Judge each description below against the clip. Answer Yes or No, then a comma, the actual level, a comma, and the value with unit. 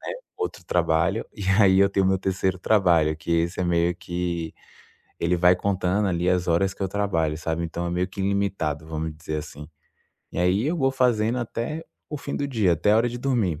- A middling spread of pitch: Yes, average, 3.6 semitones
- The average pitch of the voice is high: No, very low, 90 Hz